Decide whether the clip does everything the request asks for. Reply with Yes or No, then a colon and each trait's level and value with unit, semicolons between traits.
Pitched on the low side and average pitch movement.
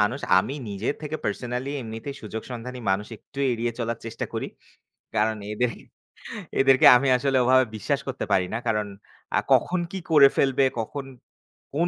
Yes: low, 125 Hz; average, 3.6 semitones